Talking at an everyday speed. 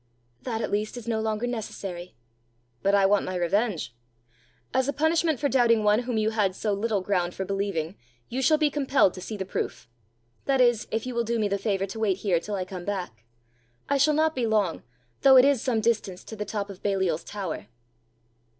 No: fast, 215 wpm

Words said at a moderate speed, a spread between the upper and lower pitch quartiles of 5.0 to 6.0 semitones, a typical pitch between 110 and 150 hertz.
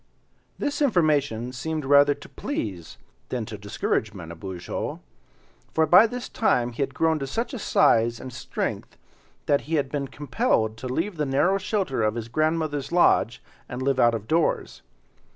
Yes: average, 165 wpm; wide, 5.6 semitones; medium, 140 Hz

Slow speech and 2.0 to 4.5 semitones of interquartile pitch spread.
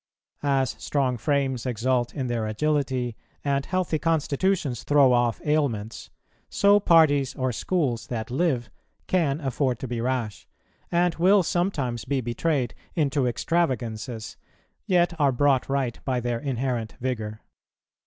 Yes: slow, 130 wpm; average, 3.9 semitones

